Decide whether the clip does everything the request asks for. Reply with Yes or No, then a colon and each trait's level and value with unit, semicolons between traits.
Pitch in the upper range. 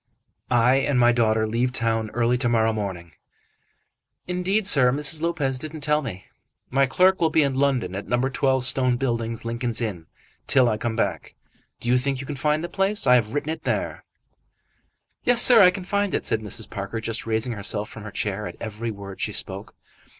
No: low, 125 Hz